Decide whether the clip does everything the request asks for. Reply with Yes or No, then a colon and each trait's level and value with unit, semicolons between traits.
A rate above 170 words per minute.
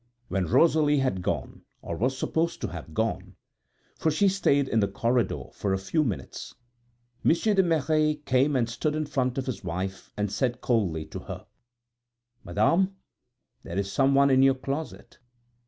No: average, 165 wpm